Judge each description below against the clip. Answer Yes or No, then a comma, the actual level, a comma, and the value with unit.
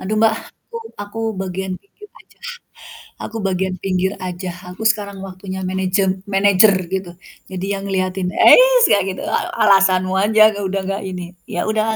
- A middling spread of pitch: No, narrow, 1.7 semitones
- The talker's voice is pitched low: No, high, 190 Hz